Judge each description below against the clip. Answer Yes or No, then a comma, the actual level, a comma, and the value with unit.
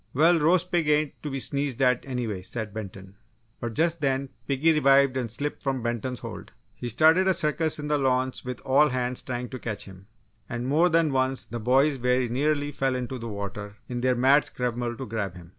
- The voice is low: Yes, low, 130 Hz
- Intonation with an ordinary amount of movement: Yes, average, 3.7 semitones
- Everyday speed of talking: No, fast, 210 wpm